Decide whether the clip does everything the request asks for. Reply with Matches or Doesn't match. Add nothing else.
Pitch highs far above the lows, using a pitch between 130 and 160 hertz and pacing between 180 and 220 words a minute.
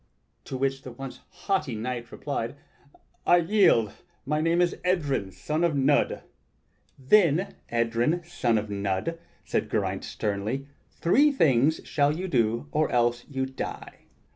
Doesn't match